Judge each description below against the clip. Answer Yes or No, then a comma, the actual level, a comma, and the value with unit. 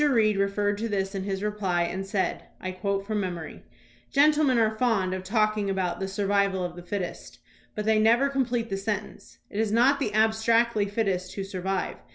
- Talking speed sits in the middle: Yes, average, 190 wpm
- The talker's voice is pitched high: Yes, high, 205 Hz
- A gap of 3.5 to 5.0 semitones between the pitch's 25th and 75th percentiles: No, narrow, 2.6 semitones